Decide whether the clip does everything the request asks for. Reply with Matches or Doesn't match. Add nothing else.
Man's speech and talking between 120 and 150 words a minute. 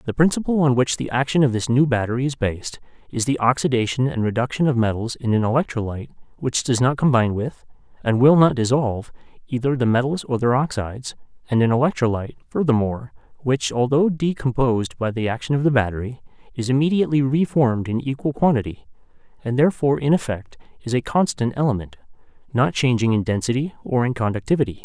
Doesn't match